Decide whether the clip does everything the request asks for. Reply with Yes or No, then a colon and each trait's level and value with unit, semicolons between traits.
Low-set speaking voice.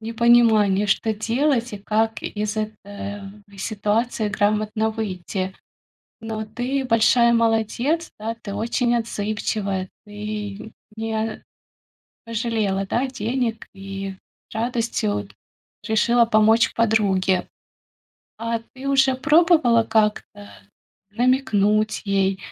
No: high, 220 Hz